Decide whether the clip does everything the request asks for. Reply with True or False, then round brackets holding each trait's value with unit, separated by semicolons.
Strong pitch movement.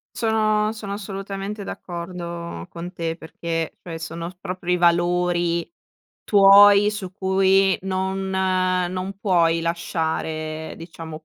False (2.5 semitones)